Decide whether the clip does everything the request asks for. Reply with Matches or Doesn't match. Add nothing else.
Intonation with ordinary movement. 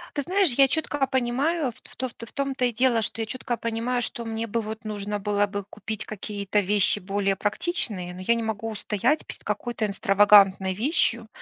Matches